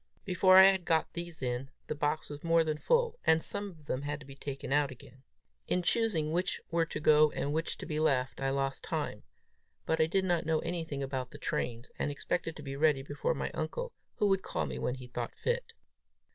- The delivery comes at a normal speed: No, fast, 225 wpm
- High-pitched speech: No, medium, 155 Hz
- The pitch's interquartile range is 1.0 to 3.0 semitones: No, average, 3.7 semitones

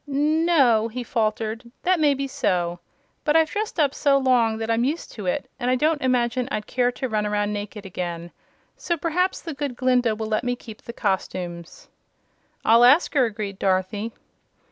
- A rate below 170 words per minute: No, average, 190 wpm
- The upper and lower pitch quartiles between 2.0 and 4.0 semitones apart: No, average, 4.8 semitones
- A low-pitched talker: No, high, 240 Hz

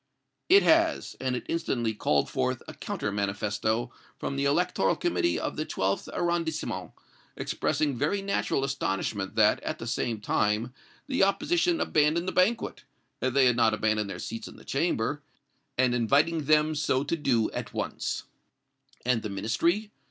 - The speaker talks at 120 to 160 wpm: Yes, average, 155 wpm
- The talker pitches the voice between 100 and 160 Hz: Yes, low, 135 Hz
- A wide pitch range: Yes, wide, 7.2 semitones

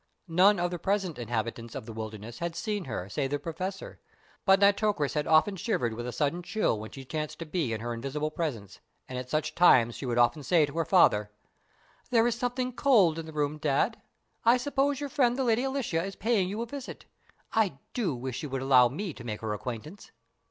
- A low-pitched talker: No, medium, 160 Hz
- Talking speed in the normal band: No, fast, 215 wpm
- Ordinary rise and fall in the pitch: No, wide, 8.7 semitones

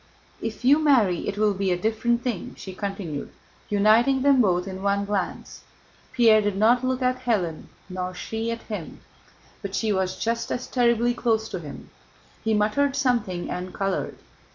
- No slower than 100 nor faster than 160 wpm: No, average, 170 wpm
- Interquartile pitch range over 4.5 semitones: No, average, 4.0 semitones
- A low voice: No, high, 215 Hz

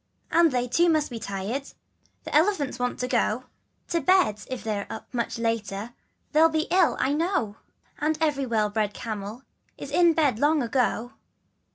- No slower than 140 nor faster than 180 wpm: Yes, average, 175 wpm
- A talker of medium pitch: No, very high, 255 Hz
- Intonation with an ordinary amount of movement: No, wide, 5.9 semitones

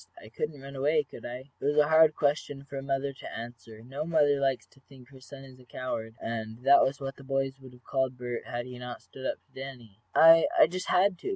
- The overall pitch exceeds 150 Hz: No, low, 135 Hz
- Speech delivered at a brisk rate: Yes, fast, 250 wpm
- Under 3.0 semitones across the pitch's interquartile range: Yes, narrow, 2.5 semitones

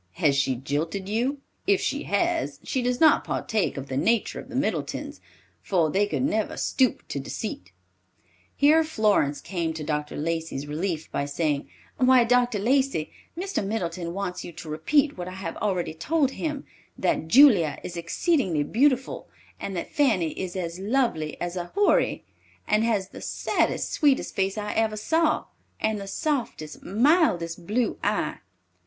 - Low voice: No, high, 200 Hz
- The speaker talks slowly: No, average, 160 wpm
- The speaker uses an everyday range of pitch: No, wide, 7.5 semitones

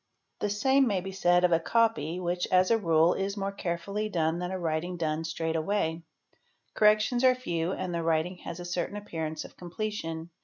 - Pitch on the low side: No, medium, 180 Hz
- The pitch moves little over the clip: No, average, 3.8 semitones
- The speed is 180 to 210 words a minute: Yes, average, 200 wpm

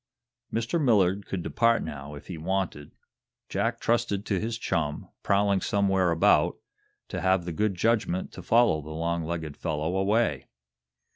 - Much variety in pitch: No, average, 4.6 semitones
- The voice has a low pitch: Yes, very low, 95 Hz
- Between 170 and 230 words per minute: No, average, 150 wpm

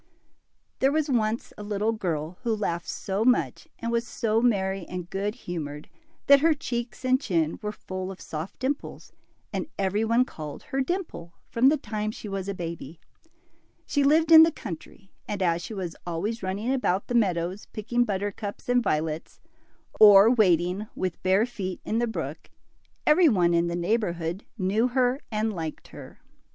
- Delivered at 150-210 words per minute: Yes, average, 175 wpm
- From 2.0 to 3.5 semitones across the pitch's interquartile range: No, average, 5.1 semitones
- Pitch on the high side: Yes, high, 210 Hz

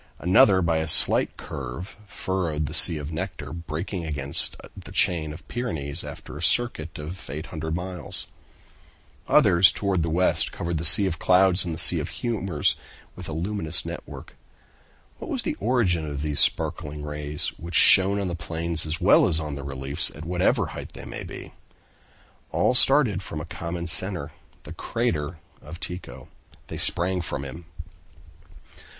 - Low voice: Yes, very low, 85 Hz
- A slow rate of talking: No, average, 165 wpm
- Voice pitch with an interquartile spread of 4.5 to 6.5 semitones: No, average, 3.4 semitones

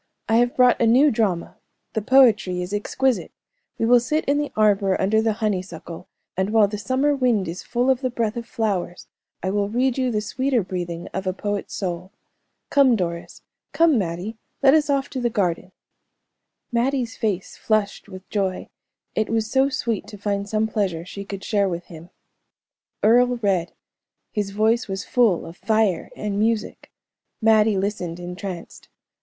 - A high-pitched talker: Yes, high, 210 Hz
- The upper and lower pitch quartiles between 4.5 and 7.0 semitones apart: No, average, 4.1 semitones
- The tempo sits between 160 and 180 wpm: Yes, average, 170 wpm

